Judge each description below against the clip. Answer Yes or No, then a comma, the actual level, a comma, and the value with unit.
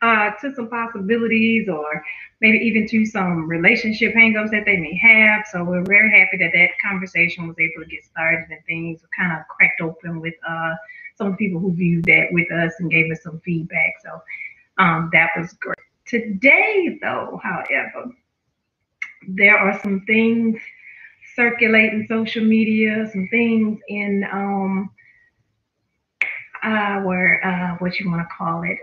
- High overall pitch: Yes, high, 195 Hz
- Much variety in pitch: No, average, 4.7 semitones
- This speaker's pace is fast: No, average, 155 wpm